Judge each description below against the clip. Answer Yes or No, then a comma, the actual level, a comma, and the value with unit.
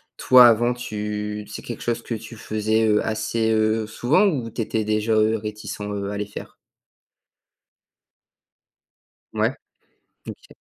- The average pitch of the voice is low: Yes, low, 110 Hz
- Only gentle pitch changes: Yes, narrow, 1.5 semitones